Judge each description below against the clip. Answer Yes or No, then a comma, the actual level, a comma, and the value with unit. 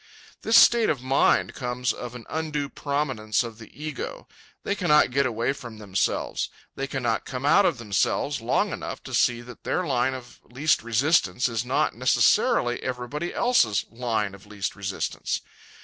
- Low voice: Yes, low, 125 Hz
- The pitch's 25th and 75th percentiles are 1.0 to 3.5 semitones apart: No, average, 3.9 semitones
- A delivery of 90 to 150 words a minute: No, average, 165 wpm